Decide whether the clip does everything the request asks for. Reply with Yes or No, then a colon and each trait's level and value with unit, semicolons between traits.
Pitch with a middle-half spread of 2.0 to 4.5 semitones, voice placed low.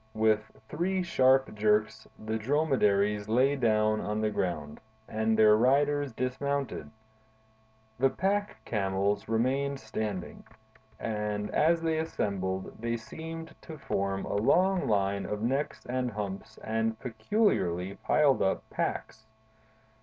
No: average, 5.1 semitones; low, 110 Hz